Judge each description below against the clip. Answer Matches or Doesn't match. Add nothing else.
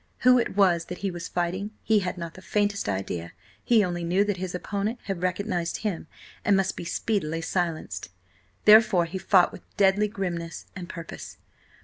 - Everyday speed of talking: Matches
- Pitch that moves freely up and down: Doesn't match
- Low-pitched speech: Doesn't match